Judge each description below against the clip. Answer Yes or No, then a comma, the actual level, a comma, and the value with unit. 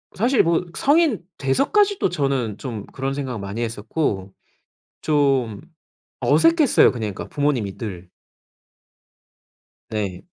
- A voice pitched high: No, low, 135 Hz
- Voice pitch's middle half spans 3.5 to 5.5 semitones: No, wide, 8.1 semitones